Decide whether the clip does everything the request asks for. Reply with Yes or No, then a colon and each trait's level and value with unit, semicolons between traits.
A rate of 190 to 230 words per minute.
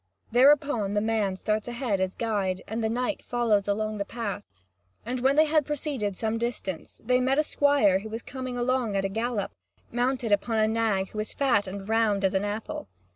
Yes: fast, 205 wpm